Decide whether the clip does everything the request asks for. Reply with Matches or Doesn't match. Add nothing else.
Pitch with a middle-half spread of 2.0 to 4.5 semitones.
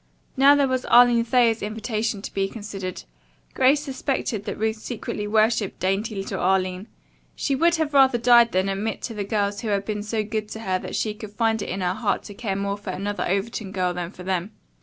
Matches